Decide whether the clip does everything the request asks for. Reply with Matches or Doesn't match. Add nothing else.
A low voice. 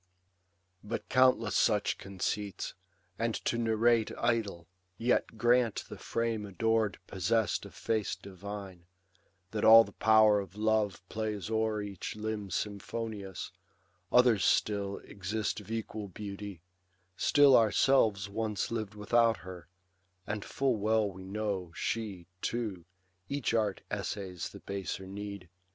Matches